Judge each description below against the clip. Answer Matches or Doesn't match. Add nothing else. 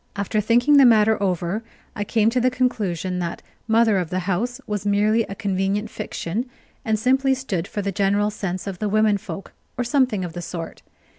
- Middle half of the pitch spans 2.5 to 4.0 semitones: Matches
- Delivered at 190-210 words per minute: Matches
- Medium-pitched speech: Doesn't match